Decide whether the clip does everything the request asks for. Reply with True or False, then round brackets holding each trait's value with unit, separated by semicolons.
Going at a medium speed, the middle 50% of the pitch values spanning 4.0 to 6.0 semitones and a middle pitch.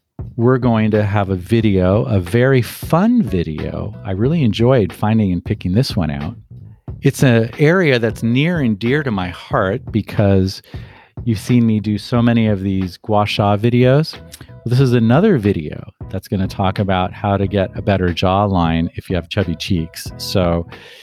False (180 wpm; 4.4 semitones; 110 Hz)